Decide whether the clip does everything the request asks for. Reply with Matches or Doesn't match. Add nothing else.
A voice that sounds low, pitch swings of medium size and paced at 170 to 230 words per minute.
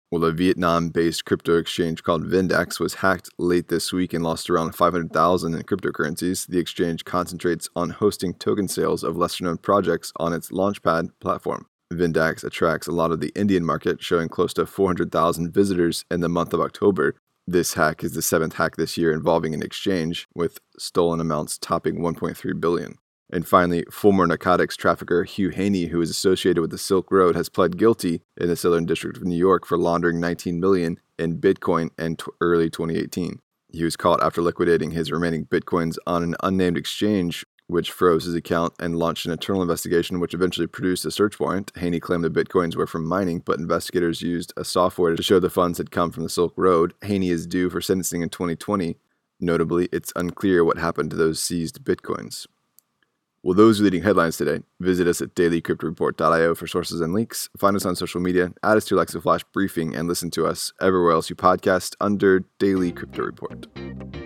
Doesn't match